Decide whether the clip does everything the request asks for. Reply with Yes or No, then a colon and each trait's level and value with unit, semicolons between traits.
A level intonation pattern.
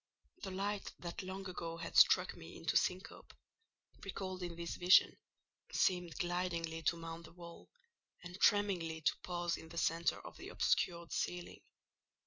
Yes: narrow, 1.7 semitones